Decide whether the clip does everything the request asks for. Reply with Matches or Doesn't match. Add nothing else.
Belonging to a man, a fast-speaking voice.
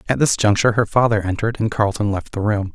Matches